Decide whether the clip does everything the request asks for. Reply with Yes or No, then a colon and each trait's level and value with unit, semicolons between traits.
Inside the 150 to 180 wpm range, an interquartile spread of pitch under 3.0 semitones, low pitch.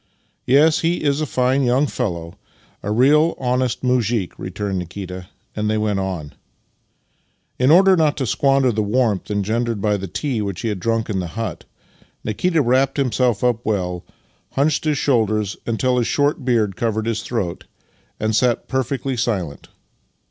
No: average, 165 wpm; average, 4.4 semitones; low, 115 Hz